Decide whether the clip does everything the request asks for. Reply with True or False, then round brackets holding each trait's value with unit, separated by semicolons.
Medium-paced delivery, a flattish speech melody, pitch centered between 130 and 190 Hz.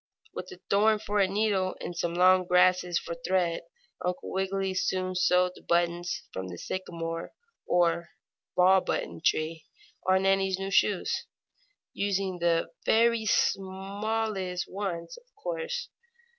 False (130 wpm; 2.3 semitones; 185 Hz)